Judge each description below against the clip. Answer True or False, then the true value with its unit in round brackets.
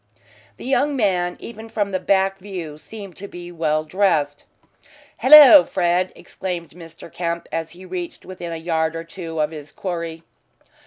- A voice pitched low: False (175 Hz)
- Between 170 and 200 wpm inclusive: False (160 wpm)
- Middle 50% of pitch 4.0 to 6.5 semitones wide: False (3.0 semitones)